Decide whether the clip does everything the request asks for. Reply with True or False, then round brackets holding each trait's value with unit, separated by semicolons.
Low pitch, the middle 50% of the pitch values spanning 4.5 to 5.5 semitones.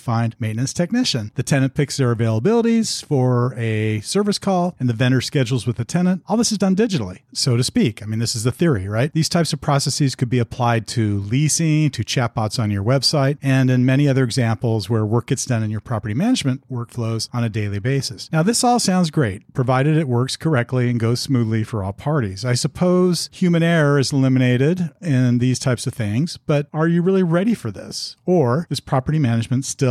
True (130 Hz; 4.9 semitones)